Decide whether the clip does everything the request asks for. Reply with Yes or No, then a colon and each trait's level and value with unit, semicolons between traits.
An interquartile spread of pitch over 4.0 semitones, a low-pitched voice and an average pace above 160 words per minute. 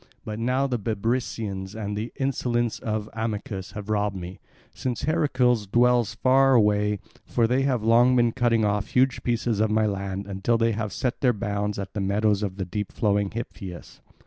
No: average, 3.0 semitones; low, 110 Hz; average, 175 wpm